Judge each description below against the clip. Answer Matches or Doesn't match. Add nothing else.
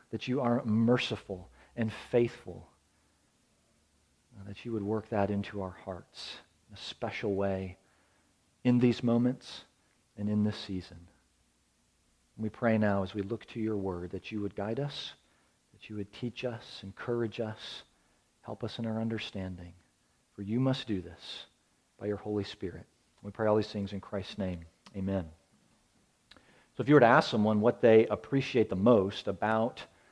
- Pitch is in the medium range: Doesn't match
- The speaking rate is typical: Matches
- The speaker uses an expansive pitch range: Doesn't match